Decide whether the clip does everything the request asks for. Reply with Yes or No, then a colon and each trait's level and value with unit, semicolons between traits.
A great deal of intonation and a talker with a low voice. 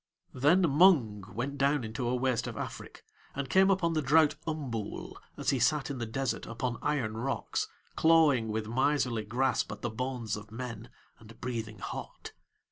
No: average, 4.3 semitones; low, 125 Hz